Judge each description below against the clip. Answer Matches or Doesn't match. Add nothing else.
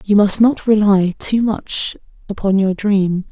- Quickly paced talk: Doesn't match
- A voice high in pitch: Matches